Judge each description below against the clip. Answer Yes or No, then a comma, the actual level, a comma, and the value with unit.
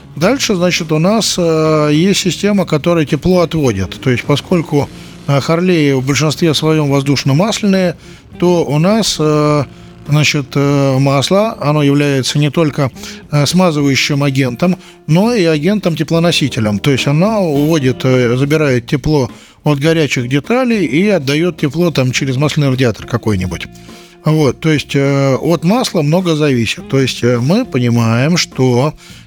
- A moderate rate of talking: Yes, average, 125 wpm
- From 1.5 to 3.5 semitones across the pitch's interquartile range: No, average, 4.1 semitones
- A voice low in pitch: No, medium, 150 Hz